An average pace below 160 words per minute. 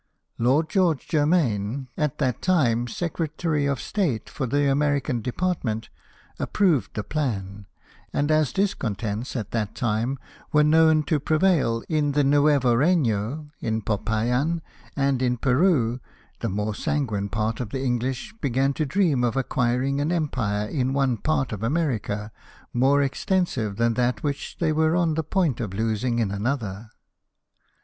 Yes: average, 150 wpm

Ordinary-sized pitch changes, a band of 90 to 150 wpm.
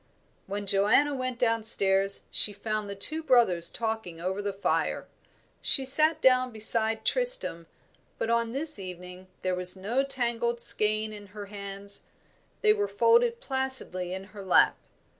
Yes: average, 4.9 semitones; average, 145 wpm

